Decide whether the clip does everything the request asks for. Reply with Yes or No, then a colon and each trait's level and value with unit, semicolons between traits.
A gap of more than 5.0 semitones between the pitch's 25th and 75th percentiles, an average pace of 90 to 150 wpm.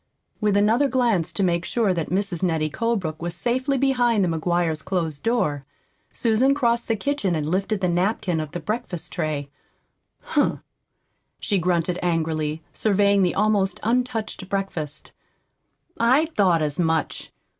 Yes: wide, 5.6 semitones; average, 145 wpm